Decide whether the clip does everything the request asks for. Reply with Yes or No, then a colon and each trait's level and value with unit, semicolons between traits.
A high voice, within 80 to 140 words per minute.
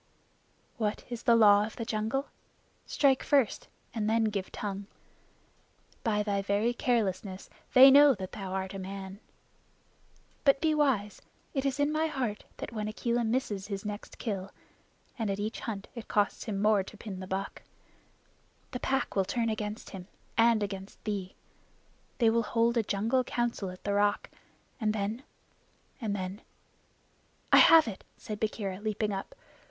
No: high, 215 Hz; average, 160 wpm